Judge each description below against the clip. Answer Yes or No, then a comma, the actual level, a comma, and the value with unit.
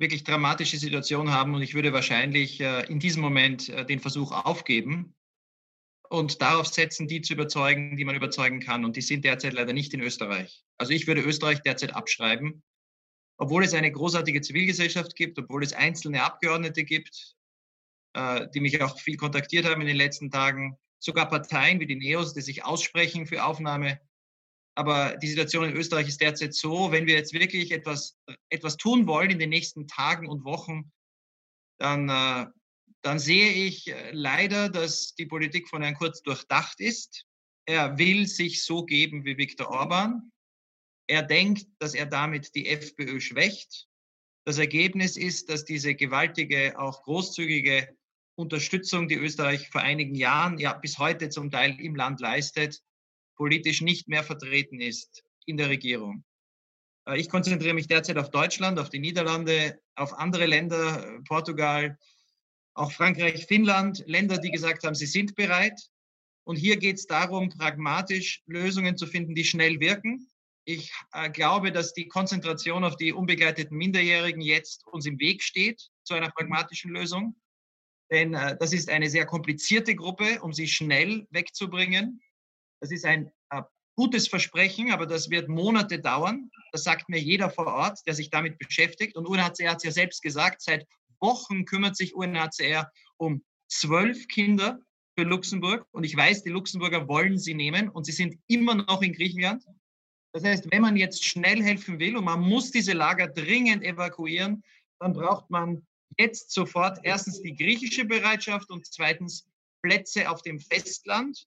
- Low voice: No, medium, 165 Hz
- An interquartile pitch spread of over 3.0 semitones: Yes, average, 3.7 semitones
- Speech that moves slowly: No, average, 160 wpm